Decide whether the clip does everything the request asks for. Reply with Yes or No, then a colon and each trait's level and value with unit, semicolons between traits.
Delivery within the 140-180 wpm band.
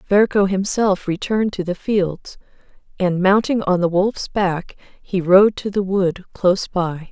Yes: average, 160 wpm